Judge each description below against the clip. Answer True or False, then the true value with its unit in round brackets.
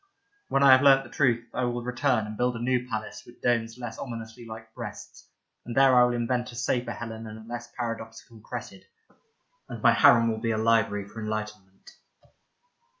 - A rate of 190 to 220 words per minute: True (200 wpm)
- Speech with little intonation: True (1.8 semitones)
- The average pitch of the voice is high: False (115 Hz)